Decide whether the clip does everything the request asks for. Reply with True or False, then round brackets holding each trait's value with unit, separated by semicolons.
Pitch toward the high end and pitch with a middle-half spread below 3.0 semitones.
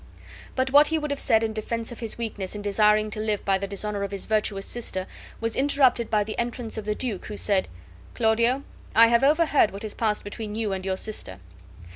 True (220 Hz; 2.5 semitones)